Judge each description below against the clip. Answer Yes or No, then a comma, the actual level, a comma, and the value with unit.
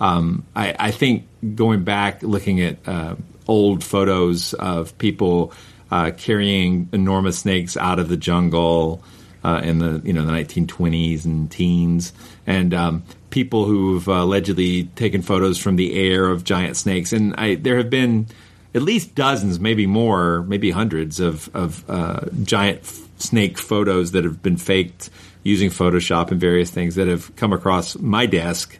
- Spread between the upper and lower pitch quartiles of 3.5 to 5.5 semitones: No, average, 2.8 semitones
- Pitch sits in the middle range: No, very low, 90 Hz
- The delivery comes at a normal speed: Yes, average, 160 wpm